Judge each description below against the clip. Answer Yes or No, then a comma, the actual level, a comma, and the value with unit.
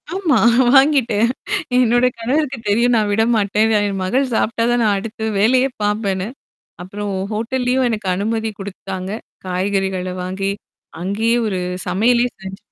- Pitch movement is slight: No, average, 3.7 semitones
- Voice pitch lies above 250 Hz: No, high, 220 Hz